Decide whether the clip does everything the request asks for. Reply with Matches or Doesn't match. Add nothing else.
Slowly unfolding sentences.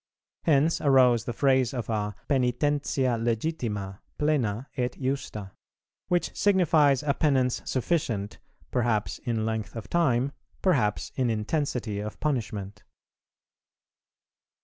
Matches